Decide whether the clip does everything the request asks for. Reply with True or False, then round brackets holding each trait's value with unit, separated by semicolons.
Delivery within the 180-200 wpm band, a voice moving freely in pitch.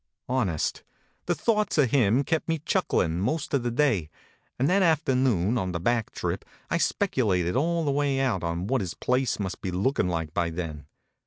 True (190 wpm; 7.9 semitones)